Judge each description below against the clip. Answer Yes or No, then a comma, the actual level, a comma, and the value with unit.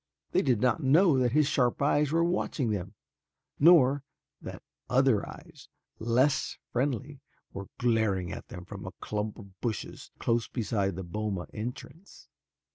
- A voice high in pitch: No, low, 120 Hz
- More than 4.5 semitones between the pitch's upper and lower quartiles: Yes, average, 5.2 semitones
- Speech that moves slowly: No, average, 145 wpm